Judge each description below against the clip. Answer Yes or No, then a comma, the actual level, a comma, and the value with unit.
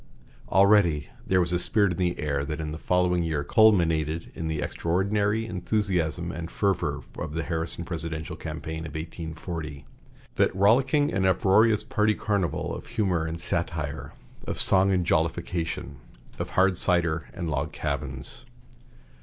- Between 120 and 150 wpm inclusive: Yes, average, 145 wpm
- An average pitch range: Yes, average, 3.4 semitones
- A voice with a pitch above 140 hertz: No, very low, 85 Hz